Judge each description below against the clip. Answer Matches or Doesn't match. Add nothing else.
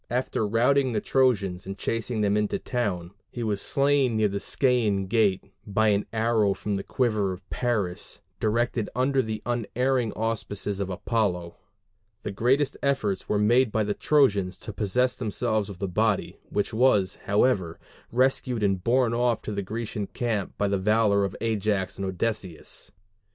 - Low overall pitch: Matches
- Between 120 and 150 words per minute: Doesn't match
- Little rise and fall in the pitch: Doesn't match